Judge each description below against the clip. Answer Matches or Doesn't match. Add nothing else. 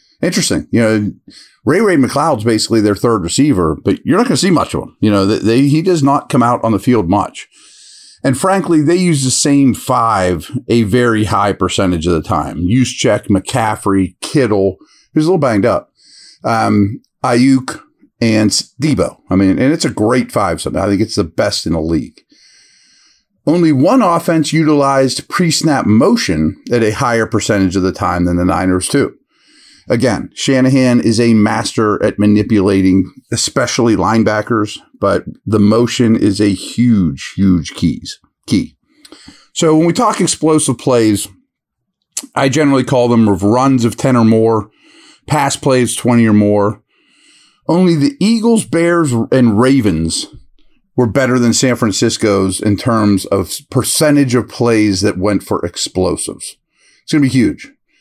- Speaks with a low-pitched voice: Matches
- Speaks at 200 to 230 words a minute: Doesn't match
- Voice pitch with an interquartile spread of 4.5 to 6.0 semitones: Matches